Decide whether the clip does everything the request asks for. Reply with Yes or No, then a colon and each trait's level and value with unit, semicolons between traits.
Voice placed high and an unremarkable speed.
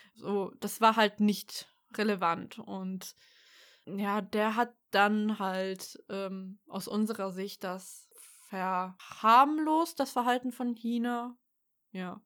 No: high, 210 Hz; slow, 115 wpm